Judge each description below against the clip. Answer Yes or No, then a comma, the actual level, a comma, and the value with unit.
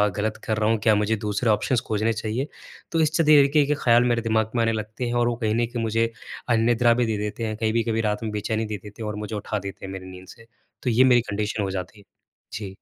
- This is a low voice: Yes, low, 110 Hz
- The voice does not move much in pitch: Yes, narrow, 2.0 semitones